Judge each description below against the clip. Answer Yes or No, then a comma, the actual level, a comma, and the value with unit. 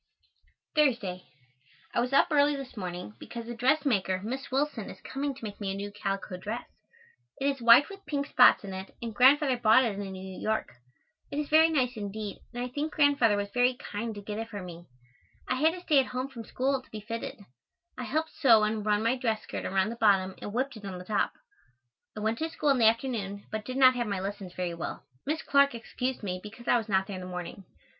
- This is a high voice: Yes, high, 230 Hz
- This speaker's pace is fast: Yes, fast, 230 wpm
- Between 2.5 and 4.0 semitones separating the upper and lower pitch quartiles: No, average, 4.8 semitones